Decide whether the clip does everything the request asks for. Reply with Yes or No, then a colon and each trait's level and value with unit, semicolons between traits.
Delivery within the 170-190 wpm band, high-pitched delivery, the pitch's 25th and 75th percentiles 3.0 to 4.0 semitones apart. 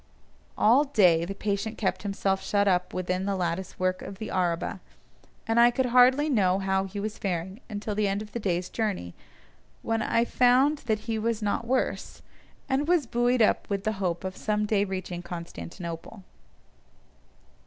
Yes: average, 175 wpm; high, 205 Hz; average, 3.6 semitones